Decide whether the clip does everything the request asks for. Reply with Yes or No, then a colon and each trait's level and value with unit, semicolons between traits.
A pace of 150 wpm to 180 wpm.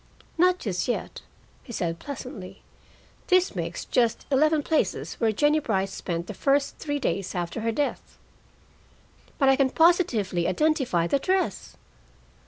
No: average, 140 wpm